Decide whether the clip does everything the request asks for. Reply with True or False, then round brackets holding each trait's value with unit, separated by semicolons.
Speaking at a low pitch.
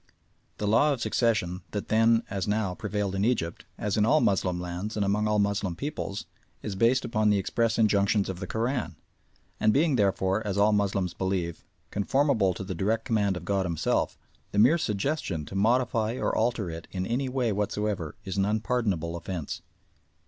True (105 Hz)